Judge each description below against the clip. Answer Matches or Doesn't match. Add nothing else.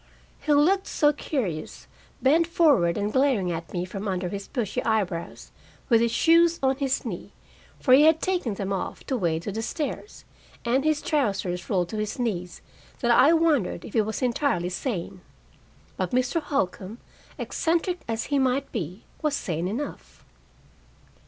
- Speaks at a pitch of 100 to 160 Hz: Doesn't match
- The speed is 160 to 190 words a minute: Matches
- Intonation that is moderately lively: Doesn't match